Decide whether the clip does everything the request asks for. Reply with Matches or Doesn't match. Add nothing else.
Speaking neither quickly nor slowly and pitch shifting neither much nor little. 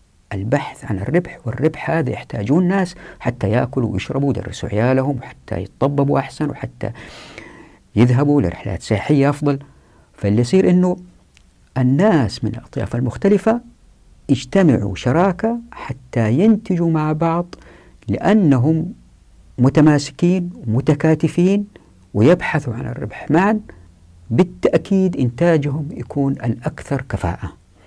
Doesn't match